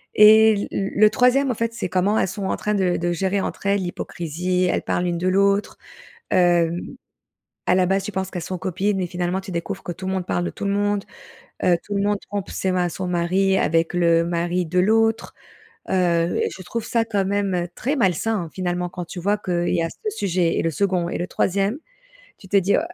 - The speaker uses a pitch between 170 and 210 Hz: Yes, high, 190 Hz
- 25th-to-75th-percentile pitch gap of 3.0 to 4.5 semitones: No, narrow, 2.5 semitones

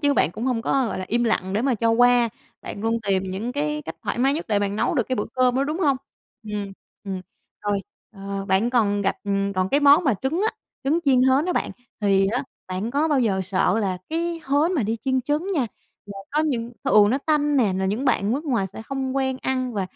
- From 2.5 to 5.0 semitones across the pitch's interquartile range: No, wide, 5.5 semitones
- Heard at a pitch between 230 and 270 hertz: Yes, high, 245 Hz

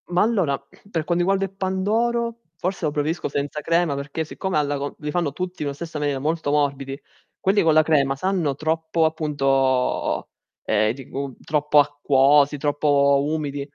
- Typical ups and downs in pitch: Yes, average, 3.6 semitones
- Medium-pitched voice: Yes, medium, 150 Hz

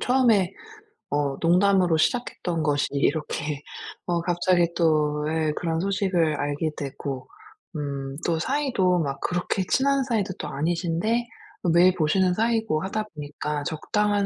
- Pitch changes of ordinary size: Yes, average, 4.7 semitones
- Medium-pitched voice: Yes, medium, 170 Hz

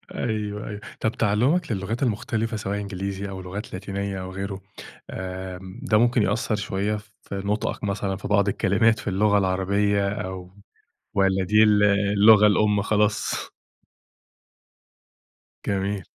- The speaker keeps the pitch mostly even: Yes, narrow, 1.6 semitones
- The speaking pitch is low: Yes, low, 100 Hz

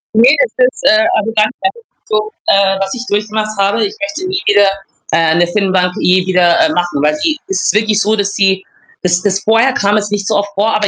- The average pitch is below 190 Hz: No, high, 205 Hz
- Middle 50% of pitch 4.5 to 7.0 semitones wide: No, average, 2.8 semitones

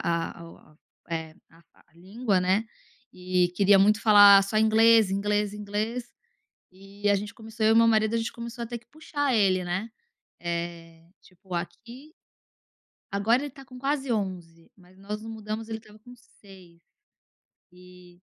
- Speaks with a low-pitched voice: No, high, 205 Hz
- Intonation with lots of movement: No, average, 3.8 semitones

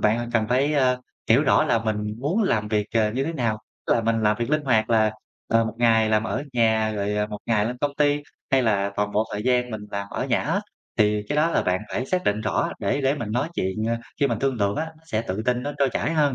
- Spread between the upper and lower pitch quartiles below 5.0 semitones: Yes, average, 4.0 semitones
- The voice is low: Yes, low, 115 Hz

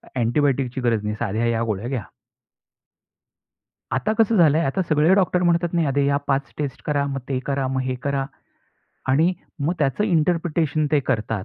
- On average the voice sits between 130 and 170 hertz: Yes, medium, 140 Hz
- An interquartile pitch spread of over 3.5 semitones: Yes, average, 4.1 semitones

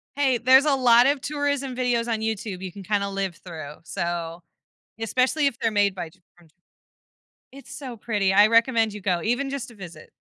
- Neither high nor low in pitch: No, high, 225 Hz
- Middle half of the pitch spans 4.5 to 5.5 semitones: Yes, average, 5.2 semitones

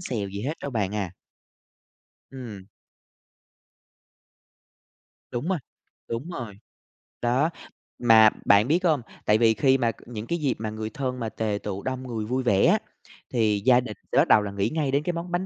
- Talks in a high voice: No, low, 120 Hz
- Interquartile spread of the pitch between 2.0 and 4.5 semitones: Yes, average, 4.2 semitones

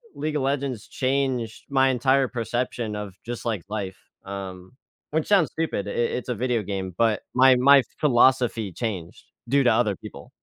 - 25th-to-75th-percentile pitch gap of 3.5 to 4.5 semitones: Yes, average, 4.2 semitones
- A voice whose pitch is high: No, low, 120 Hz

